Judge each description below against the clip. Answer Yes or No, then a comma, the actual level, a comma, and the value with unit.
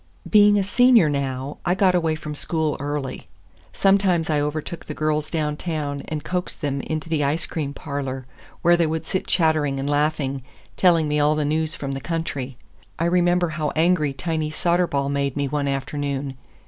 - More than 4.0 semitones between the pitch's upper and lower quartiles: No, average, 3.0 semitones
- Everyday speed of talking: Yes, average, 175 wpm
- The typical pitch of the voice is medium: Yes, medium, 155 Hz